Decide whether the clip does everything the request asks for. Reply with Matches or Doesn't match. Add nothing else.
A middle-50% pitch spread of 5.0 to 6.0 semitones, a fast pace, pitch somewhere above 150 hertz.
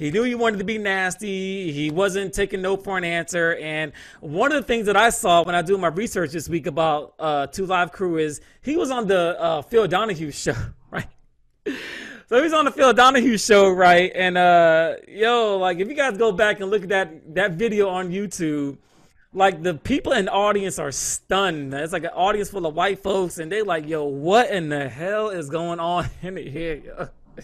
Doesn't match